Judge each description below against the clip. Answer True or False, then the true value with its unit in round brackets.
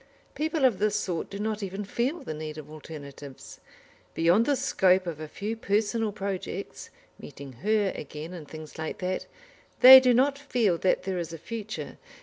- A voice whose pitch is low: False (195 Hz)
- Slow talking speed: False (175 wpm)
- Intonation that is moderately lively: False (6.0 semitones)